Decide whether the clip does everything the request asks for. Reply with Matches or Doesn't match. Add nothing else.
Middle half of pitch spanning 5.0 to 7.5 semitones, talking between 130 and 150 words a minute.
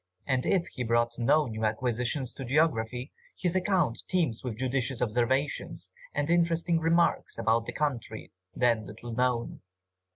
Matches